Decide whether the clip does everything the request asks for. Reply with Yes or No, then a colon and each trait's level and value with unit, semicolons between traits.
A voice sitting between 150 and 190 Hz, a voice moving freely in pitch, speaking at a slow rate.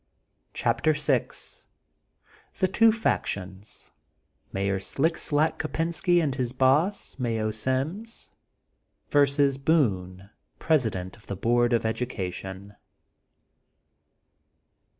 No: low, 130 Hz; wide, 7.4 semitones; slow, 90 wpm